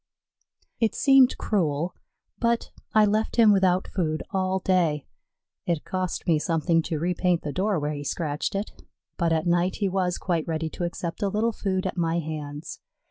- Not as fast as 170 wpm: No, average, 175 wpm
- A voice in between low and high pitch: Yes, medium, 180 Hz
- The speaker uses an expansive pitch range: No, average, 3.3 semitones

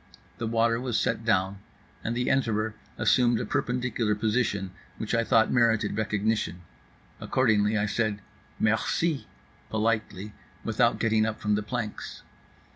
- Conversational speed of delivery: No, slow, 130 wpm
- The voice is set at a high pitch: No, low, 110 Hz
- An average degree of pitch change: No, narrow, 1.8 semitones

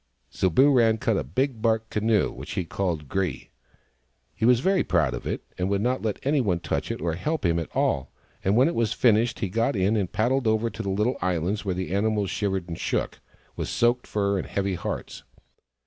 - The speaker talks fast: Yes, fast, 210 wpm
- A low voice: Yes, low, 105 Hz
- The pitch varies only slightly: No, average, 4.1 semitones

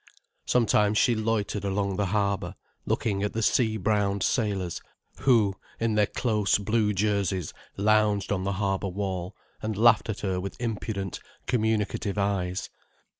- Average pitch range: No, narrow, 1.9 semitones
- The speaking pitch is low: Yes, low, 105 Hz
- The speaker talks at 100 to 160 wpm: Yes, average, 140 wpm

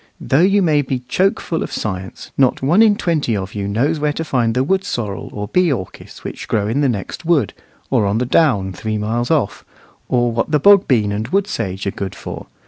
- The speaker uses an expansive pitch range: Yes, wide, 7.4 semitones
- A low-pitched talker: Yes, low, 125 Hz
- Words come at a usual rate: No, fast, 225 wpm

